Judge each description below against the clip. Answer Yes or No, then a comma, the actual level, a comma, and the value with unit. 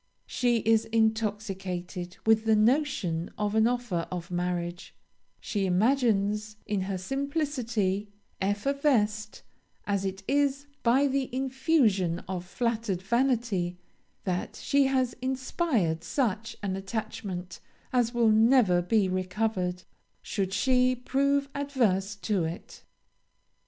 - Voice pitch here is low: No, high, 215 Hz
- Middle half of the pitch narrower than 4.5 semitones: No, average, 5.1 semitones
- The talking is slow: Yes, slow, 110 wpm